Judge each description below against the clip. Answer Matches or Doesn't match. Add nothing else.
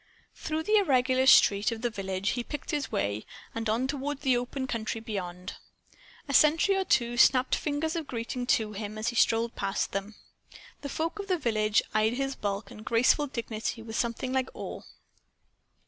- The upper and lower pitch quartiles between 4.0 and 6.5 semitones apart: Matches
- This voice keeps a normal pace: Matches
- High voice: Matches